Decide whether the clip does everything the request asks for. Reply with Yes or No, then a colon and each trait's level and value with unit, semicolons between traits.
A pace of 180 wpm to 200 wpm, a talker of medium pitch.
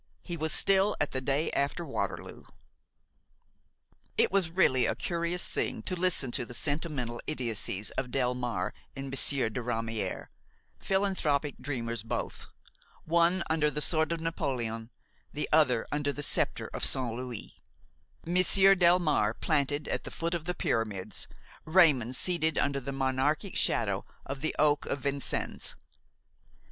No: average, 140 wpm; medium, 145 Hz